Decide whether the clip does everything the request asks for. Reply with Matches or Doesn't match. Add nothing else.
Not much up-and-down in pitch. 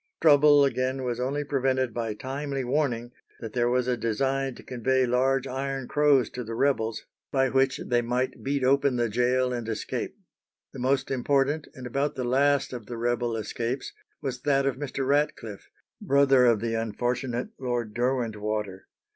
Matches